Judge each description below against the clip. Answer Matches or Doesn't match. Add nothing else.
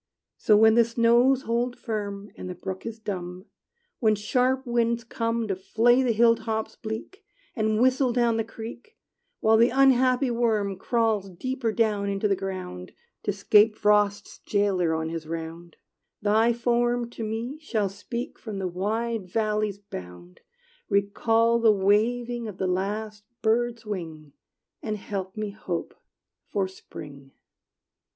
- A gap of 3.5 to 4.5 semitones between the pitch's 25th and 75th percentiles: Doesn't match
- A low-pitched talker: Doesn't match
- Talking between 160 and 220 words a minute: Doesn't match